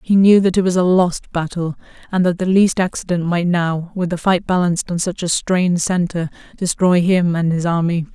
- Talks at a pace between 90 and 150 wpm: No, average, 200 wpm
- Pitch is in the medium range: Yes, medium, 175 Hz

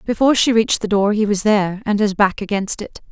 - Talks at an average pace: No, fast, 230 wpm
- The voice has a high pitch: Yes, high, 210 Hz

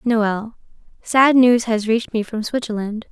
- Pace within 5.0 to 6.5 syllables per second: No, 4.3 syllables/s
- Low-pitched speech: No, high, 225 Hz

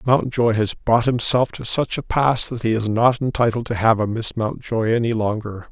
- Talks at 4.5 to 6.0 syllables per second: Yes, 4.9 syllables/s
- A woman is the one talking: No, male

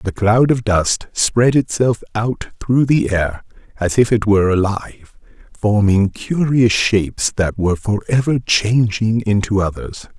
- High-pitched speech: No, low, 110 Hz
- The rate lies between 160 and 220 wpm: No, average, 145 wpm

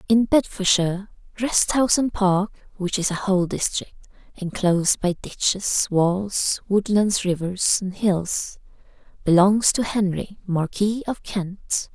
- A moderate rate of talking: No, slow, 125 wpm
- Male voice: No, female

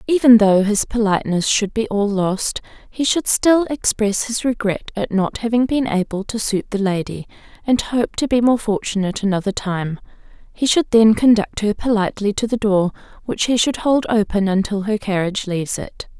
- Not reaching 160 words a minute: No, average, 185 wpm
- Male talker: No, female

